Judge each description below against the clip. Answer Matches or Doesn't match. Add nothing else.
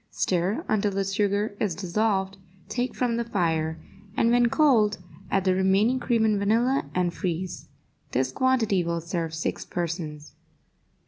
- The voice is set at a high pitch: Matches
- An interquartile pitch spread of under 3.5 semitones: Doesn't match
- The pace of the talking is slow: Doesn't match